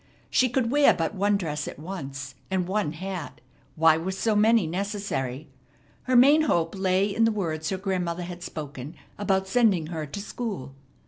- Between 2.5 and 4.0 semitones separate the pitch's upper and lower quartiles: No, average, 4.5 semitones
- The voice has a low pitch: No, medium, 185 Hz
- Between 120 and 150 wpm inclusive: No, average, 175 wpm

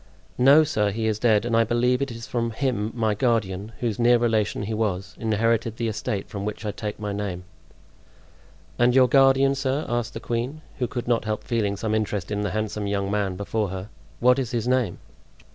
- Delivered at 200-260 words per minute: Yes, fast, 205 wpm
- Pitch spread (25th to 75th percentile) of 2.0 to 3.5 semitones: Yes, average, 2.7 semitones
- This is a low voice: Yes, low, 110 Hz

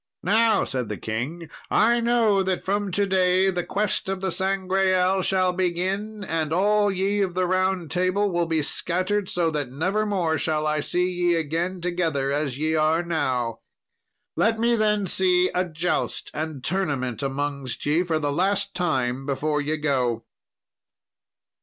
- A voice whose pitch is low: No, medium, 180 Hz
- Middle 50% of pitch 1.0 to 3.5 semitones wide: No, average, 4.0 semitones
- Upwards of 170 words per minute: No, average, 160 wpm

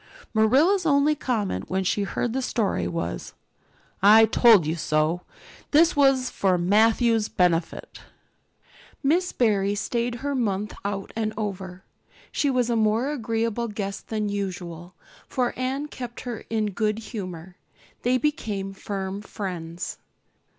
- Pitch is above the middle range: Yes, high, 215 Hz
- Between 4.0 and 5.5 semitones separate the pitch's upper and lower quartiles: Yes, average, 4.4 semitones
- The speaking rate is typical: No, slow, 130 wpm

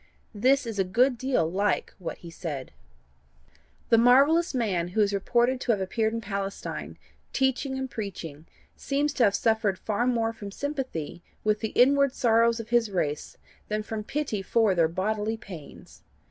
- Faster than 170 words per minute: No, average, 165 wpm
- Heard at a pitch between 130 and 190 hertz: No, high, 220 Hz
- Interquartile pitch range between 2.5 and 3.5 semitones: No, average, 4.3 semitones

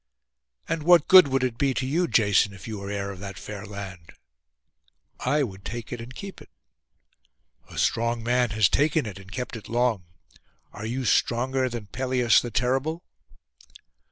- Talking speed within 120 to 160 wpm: No, average, 175 wpm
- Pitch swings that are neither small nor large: Yes, average, 4.4 semitones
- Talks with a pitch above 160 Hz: No, low, 120 Hz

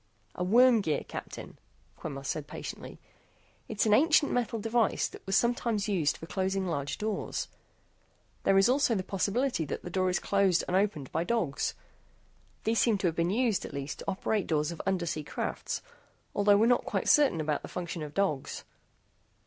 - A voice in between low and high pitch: No, high, 195 Hz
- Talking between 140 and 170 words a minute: No, average, 180 wpm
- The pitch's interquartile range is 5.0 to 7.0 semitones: Yes, average, 5.3 semitones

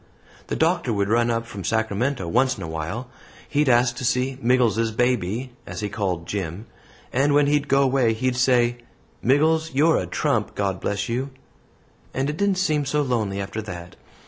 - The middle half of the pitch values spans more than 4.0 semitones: Yes, average, 4.6 semitones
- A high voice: No, low, 120 Hz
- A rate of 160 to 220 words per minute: Yes, average, 180 wpm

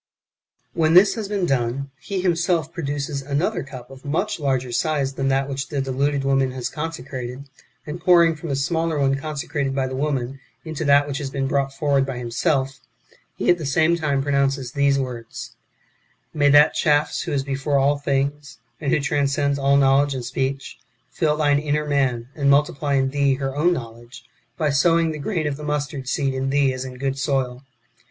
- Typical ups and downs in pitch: No, narrow, 1.9 semitones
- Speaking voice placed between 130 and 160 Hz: Yes, medium, 140 Hz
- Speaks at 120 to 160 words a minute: No, average, 190 wpm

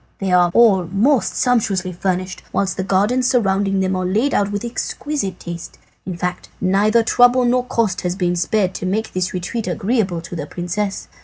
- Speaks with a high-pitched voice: Yes, high, 195 Hz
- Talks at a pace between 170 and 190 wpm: Yes, average, 180 wpm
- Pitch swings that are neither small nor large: Yes, average, 3.8 semitones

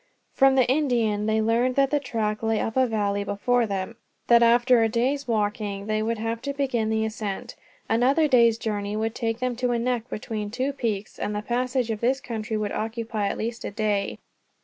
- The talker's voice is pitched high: Yes, high, 225 Hz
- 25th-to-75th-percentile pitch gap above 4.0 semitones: No, narrow, 2.6 semitones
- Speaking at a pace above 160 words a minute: Yes, average, 200 wpm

